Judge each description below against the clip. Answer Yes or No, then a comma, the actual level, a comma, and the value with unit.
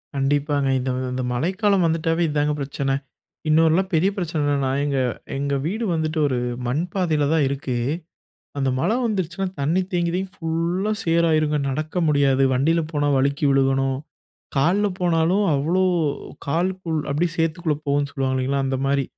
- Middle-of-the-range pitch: Yes, medium, 155 Hz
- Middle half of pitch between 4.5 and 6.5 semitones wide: No, average, 3.6 semitones